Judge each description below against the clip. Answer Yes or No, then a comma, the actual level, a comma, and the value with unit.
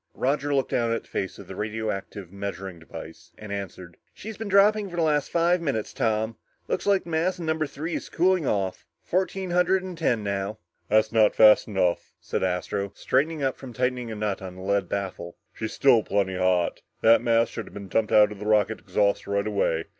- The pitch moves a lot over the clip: Yes, wide, 7.7 semitones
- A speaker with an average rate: No, fast, 210 wpm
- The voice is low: Yes, low, 110 Hz